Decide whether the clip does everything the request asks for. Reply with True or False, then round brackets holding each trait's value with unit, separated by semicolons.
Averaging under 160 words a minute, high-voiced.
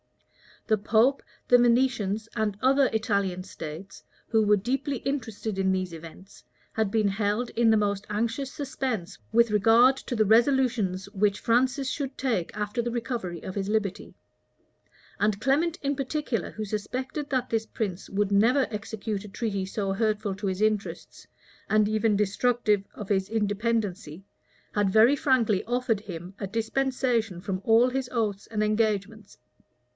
True (150 wpm; 215 Hz)